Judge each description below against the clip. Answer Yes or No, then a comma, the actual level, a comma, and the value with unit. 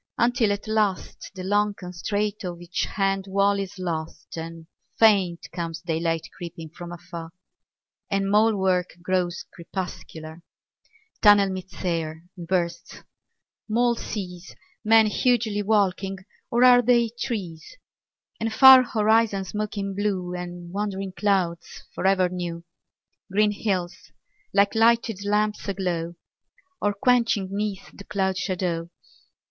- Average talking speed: No, slow, 125 wpm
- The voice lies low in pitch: No, high, 195 Hz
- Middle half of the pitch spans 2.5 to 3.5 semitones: Yes, average, 3.2 semitones